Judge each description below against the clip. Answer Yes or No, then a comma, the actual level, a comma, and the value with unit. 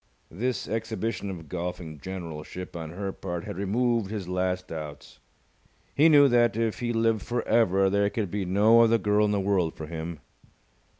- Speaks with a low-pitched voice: Yes, low, 100 Hz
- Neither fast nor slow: Yes, average, 175 wpm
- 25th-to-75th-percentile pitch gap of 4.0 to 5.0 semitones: Yes, average, 4.3 semitones